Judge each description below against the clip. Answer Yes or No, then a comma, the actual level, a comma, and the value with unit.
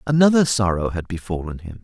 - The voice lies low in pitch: Yes, low, 110 Hz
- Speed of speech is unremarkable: Yes, average, 165 wpm